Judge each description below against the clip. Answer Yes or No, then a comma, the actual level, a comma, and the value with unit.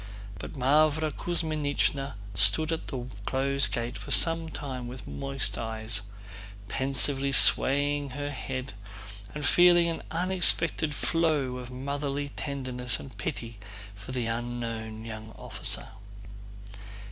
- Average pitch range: Yes, average, 3.6 semitones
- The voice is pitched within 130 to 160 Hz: Yes, low, 135 Hz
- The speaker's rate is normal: No, slow, 115 wpm